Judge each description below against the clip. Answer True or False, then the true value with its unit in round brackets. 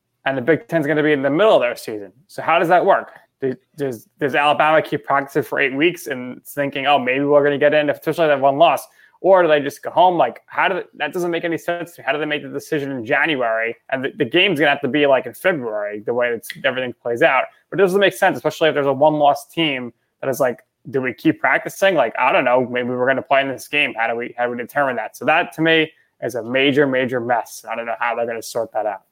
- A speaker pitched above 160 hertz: False (140 Hz)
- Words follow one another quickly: True (285 wpm)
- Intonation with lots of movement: False (3.9 semitones)